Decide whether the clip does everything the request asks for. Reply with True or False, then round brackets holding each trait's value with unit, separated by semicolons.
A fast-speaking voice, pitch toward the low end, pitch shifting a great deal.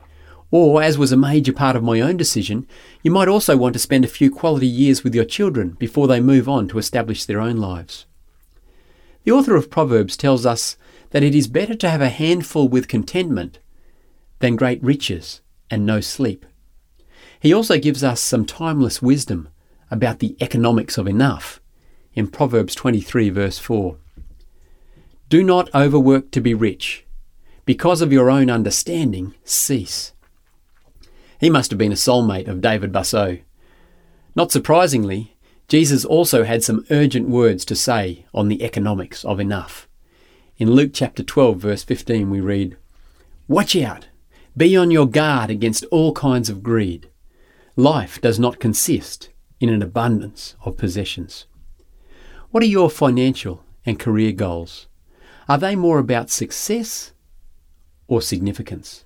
False (150 wpm; 115 Hz; 7.0 semitones)